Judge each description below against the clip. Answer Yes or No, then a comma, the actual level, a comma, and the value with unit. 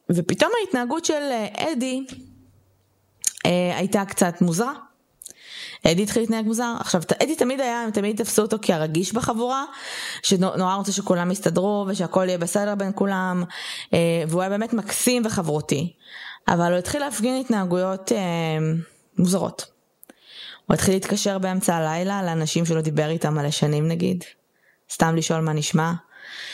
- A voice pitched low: No, high, 190 Hz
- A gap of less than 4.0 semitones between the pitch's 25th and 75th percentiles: No, average, 4.9 semitones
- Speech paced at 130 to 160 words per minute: Yes, average, 140 wpm